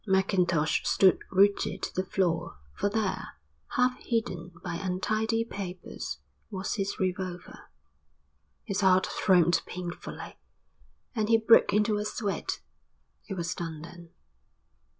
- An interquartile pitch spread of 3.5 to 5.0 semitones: No, average, 3.0 semitones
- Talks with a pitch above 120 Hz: Yes, high, 190 Hz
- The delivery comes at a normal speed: No, slow, 120 wpm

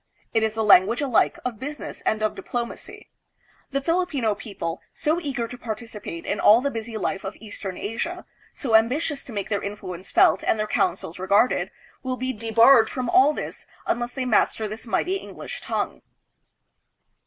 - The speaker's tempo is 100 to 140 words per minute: No, average, 170 wpm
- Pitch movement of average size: Yes, average, 3.8 semitones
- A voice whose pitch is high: Yes, high, 230 Hz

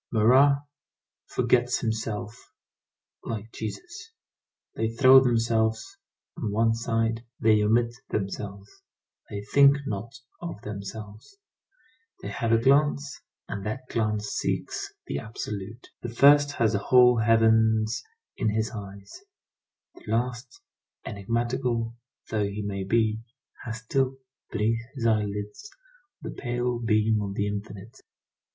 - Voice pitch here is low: Yes, low, 115 Hz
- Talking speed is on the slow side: Yes, slow, 120 wpm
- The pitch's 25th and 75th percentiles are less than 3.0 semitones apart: Yes, narrow, 2.4 semitones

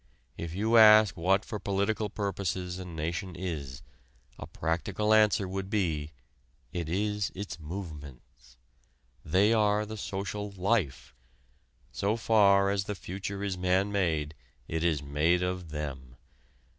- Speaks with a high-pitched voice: No, very low, 95 Hz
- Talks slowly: Yes, slow, 130 wpm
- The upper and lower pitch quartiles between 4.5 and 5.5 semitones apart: No, average, 4.0 semitones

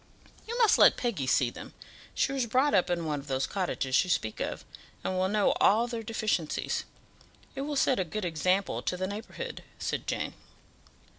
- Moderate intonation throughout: No, wide, 5.9 semitones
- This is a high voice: Yes, high, 195 Hz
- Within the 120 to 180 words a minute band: No, average, 190 wpm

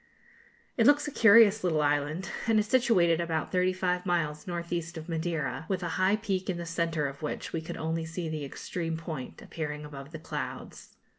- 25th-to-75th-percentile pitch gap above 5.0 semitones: No, average, 2.8 semitones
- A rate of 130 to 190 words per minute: No, average, 200 wpm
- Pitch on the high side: No, medium, 170 Hz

